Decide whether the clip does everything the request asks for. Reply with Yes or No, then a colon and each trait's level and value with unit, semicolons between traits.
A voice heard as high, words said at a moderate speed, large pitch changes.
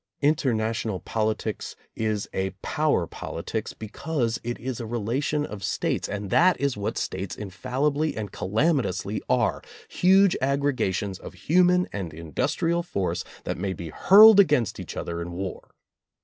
No: low, 115 Hz; average, 150 wpm; wide, 7.1 semitones